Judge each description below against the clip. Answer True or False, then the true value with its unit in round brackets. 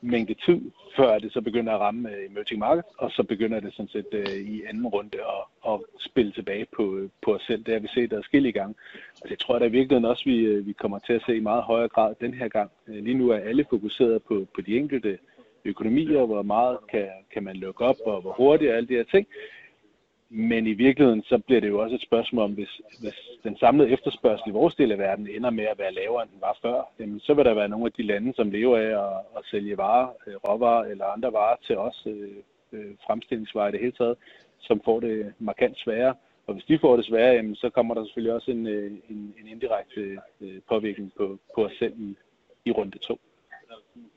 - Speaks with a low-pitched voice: True (115 Hz)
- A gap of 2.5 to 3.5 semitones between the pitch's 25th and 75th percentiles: True (2.9 semitones)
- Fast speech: True (230 wpm)